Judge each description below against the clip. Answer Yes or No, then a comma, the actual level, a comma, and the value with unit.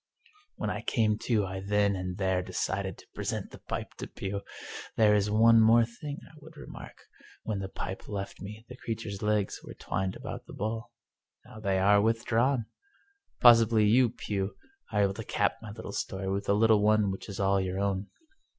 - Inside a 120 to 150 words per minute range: No, average, 195 wpm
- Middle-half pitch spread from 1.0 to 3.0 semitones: Yes, narrow, 2.4 semitones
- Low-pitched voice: Yes, low, 105 Hz